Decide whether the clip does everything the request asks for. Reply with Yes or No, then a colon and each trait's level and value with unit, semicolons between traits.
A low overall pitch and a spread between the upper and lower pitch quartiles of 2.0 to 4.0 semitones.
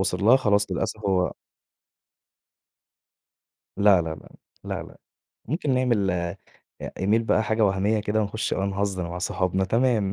Yes: low, 100 Hz; average, 2.7 semitones